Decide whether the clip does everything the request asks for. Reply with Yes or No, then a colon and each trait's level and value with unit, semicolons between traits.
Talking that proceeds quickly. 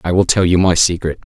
Yes: fast, 275 wpm